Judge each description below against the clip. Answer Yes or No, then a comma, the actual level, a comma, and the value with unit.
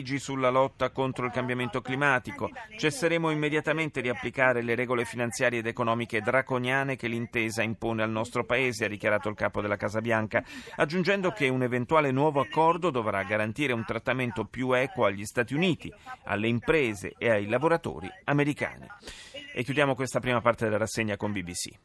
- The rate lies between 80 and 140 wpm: No, average, 160 wpm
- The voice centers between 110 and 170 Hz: Yes, low, 125 Hz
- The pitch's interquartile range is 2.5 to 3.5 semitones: Yes, average, 3.0 semitones